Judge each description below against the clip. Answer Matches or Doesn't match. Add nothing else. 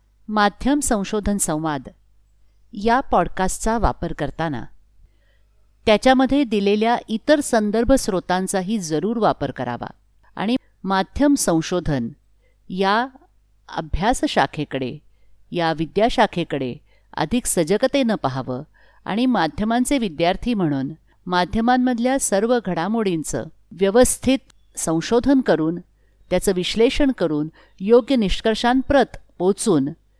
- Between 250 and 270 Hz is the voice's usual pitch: Doesn't match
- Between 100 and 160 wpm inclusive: Doesn't match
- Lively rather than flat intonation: Matches